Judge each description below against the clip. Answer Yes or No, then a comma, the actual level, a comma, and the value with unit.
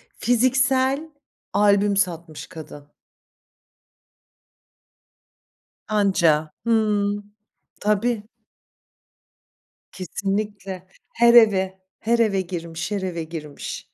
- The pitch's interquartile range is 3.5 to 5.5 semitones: Yes, average, 4.2 semitones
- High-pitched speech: Yes, high, 200 Hz